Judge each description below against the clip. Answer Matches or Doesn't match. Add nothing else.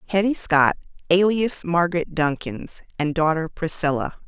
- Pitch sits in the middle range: Matches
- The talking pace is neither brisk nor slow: Doesn't match